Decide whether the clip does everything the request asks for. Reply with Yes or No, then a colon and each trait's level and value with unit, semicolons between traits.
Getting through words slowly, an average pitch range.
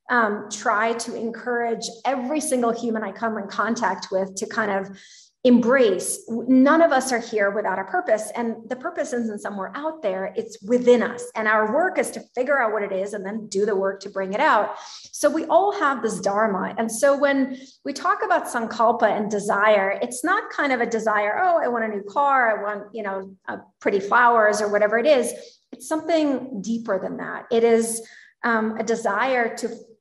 No: fast, 205 wpm; average, 3.5 semitones